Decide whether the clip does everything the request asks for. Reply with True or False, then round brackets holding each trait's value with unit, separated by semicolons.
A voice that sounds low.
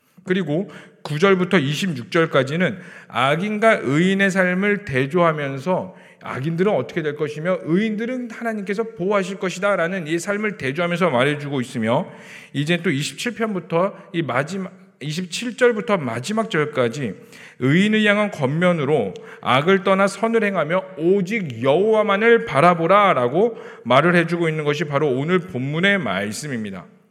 False (185 Hz)